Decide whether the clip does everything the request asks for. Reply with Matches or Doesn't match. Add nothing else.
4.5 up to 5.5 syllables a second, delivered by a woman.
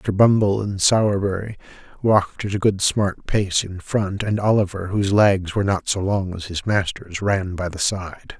Doesn't match